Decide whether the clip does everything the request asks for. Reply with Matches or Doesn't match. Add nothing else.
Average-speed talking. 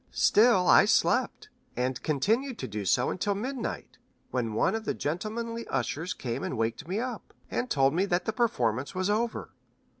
Matches